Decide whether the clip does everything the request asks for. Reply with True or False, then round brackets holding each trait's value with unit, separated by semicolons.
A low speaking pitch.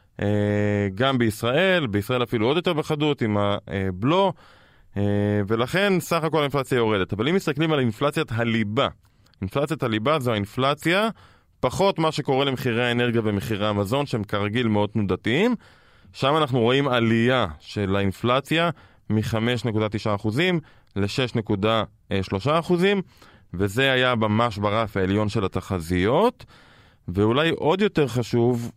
True (120 Hz)